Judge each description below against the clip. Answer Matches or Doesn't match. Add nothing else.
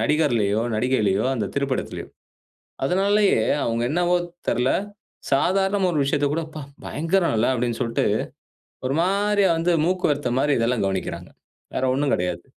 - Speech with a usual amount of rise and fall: Doesn't match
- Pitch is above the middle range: Doesn't match